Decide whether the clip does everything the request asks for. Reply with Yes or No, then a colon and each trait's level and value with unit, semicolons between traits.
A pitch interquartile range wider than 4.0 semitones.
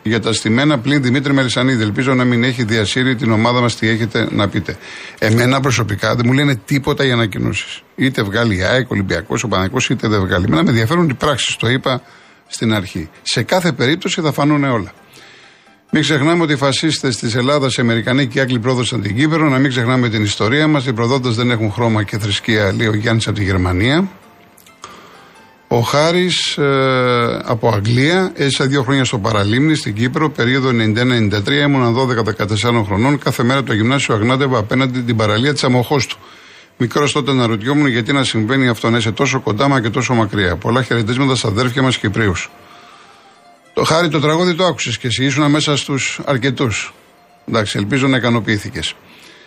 No: average, 3.7 semitones